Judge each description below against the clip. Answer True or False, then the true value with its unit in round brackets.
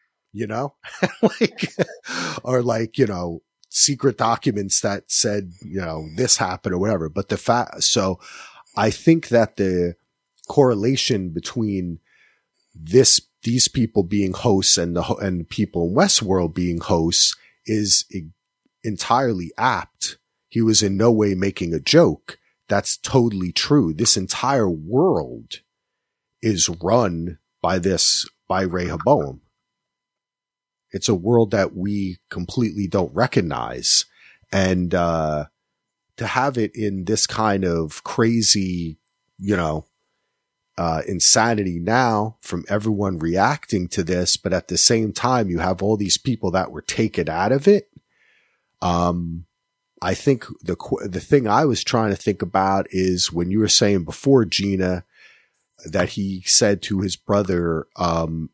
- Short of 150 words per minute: True (140 wpm)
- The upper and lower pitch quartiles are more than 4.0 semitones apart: True (4.6 semitones)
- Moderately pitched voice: False (100 Hz)